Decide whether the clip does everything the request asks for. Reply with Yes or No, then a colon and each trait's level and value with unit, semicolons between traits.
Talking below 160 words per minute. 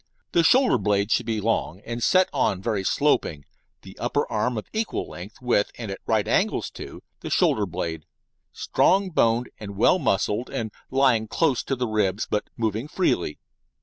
No: average, 170 wpm